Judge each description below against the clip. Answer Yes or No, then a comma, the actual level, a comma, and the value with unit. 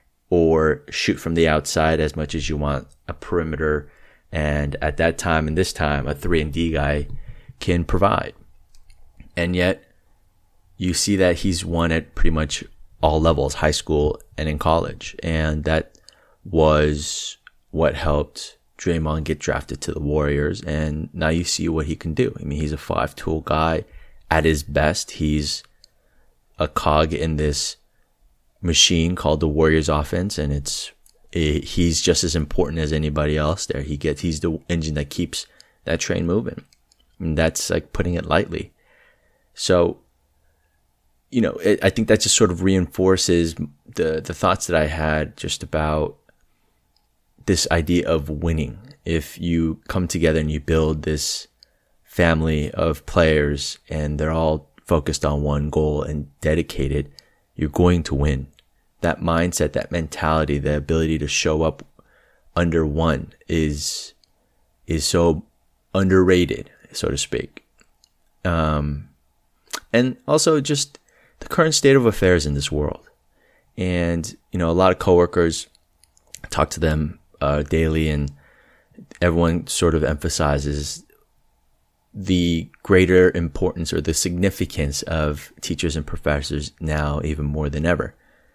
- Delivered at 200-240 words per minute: No, average, 150 wpm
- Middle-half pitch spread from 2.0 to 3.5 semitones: Yes, narrow, 2.6 semitones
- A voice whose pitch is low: Yes, very low, 80 Hz